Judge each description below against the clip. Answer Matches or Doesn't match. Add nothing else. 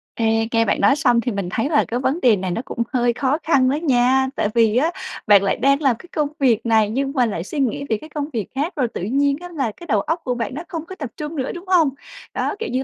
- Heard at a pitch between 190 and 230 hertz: Doesn't match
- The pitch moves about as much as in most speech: Matches